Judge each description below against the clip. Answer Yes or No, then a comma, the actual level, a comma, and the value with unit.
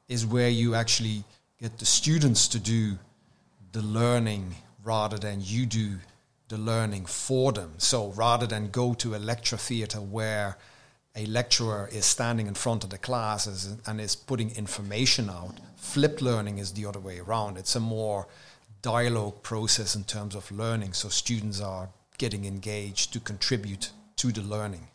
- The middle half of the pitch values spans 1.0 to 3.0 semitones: Yes, narrow, 2.4 semitones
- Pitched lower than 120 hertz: Yes, low, 110 Hz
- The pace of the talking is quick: No, average, 165 wpm